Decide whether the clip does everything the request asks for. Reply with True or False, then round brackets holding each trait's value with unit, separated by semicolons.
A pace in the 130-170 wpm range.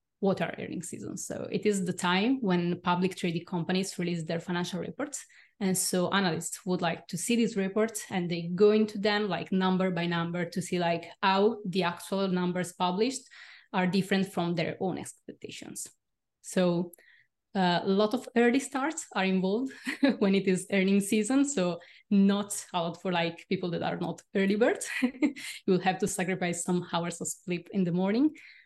False (180 wpm)